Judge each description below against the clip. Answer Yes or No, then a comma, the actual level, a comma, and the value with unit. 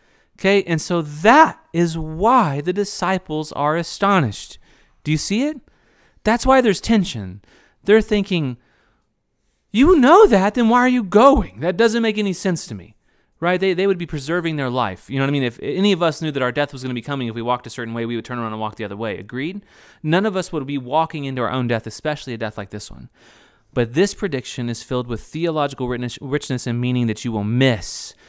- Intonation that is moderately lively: No, wide, 8.1 semitones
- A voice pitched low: No, medium, 150 Hz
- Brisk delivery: Yes, fast, 225 wpm